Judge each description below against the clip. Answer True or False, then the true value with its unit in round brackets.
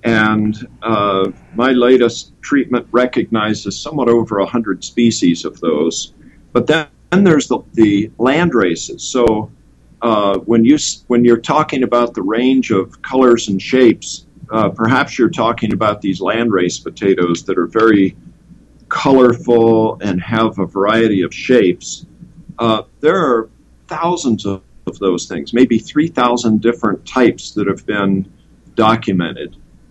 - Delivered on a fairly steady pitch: False (3.8 semitones)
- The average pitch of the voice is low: True (115 Hz)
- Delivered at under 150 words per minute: True (140 wpm)